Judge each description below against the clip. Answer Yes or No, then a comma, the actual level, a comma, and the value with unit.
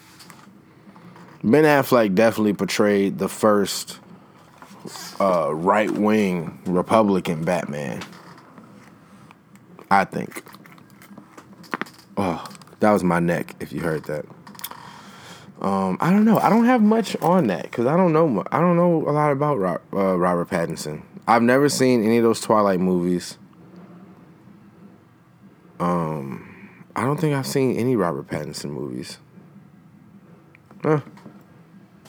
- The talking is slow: Yes, slow, 120 wpm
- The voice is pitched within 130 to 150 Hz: Yes, low, 135 Hz